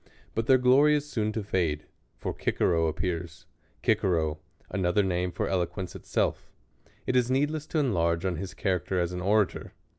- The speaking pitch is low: Yes, very low, 95 Hz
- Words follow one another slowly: No, average, 160 wpm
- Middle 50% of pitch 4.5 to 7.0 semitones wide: Yes, average, 5.3 semitones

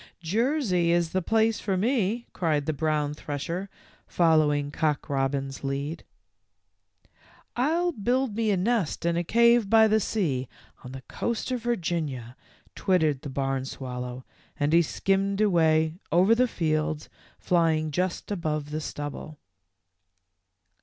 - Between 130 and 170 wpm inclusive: Yes, average, 140 wpm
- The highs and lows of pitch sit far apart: Yes, wide, 6.3 semitones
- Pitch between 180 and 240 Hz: No, medium, 165 Hz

